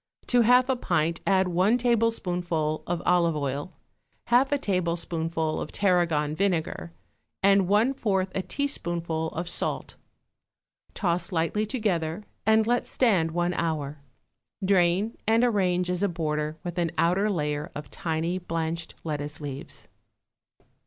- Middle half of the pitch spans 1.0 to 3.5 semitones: No, average, 4.0 semitones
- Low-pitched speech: No, medium, 175 Hz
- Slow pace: Yes, slow, 130 wpm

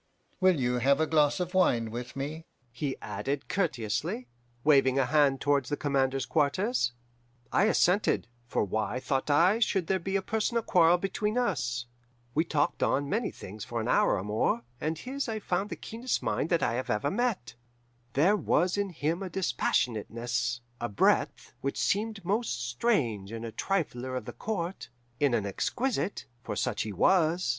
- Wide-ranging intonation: Yes, wide, 7.7 semitones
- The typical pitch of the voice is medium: Yes, medium, 150 Hz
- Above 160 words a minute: Yes, average, 175 wpm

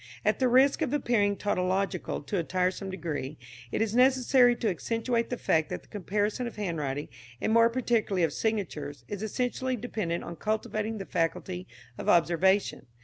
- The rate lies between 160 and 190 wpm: Yes, average, 165 wpm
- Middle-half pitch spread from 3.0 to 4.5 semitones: No, average, 5.2 semitones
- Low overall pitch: No, high, 205 Hz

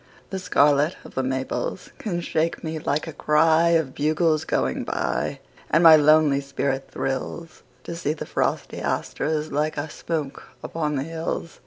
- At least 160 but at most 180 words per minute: No, average, 145 wpm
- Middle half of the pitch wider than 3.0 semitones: No, narrow, 2.4 semitones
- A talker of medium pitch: Yes, medium, 155 Hz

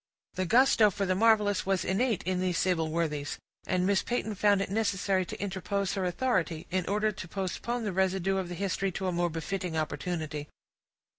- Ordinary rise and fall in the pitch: No, narrow, 2.3 semitones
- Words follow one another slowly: No, average, 190 wpm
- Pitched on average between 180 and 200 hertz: Yes, high, 190 Hz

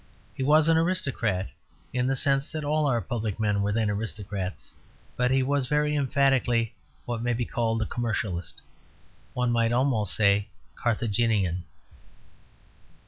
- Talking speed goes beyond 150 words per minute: No, average, 140 wpm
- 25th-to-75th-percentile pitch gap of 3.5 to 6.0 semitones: Yes, average, 4.3 semitones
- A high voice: No, low, 120 Hz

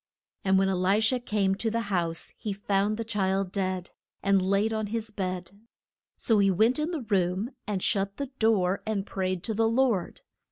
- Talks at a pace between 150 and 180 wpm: No, average, 195 wpm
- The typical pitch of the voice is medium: No, high, 200 Hz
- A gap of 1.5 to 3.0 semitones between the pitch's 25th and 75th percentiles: Yes, average, 2.7 semitones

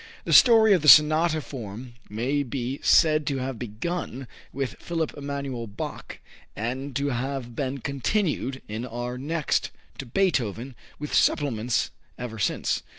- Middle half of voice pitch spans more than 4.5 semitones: No, average, 3.7 semitones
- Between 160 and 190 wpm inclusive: No, average, 140 wpm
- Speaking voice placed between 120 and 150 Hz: Yes, low, 135 Hz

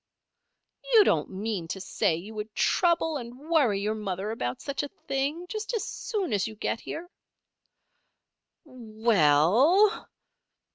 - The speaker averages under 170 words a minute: Yes, average, 140 wpm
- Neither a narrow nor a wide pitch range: No, wide, 8.3 semitones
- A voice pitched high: Yes, high, 230 Hz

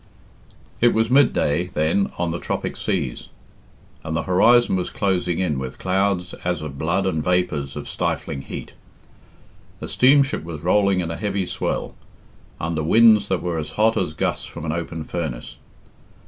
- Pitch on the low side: Yes, very low, 90 Hz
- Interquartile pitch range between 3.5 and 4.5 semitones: Yes, average, 3.8 semitones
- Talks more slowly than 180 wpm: Yes, average, 165 wpm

